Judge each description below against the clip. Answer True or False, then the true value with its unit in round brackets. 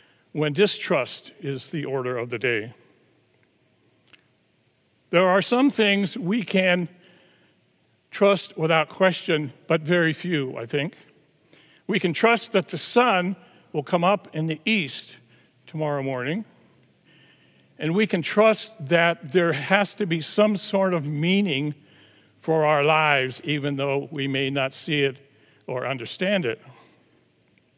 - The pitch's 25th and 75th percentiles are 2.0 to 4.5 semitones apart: False (5.4 semitones)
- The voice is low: False (160 Hz)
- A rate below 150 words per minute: True (135 wpm)